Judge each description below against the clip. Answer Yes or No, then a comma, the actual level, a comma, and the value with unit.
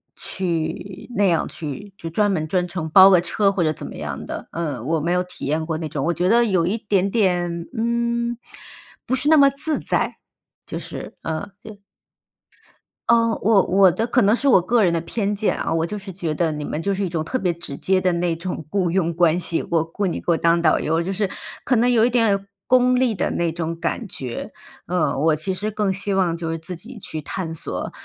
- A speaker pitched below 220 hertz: Yes, medium, 185 Hz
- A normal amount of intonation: Yes, average, 4.2 semitones